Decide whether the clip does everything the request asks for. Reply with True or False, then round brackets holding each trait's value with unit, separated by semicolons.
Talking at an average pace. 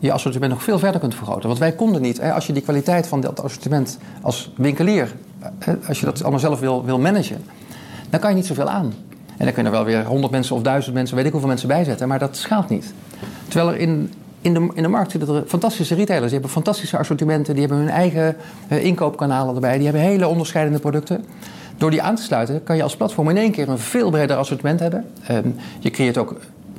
False (230 wpm)